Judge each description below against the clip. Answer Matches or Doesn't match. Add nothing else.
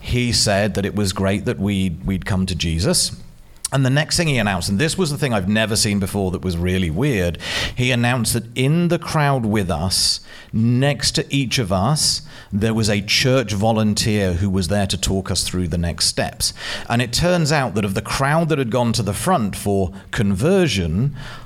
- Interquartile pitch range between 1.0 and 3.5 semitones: Doesn't match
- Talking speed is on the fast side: Matches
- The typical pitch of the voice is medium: Doesn't match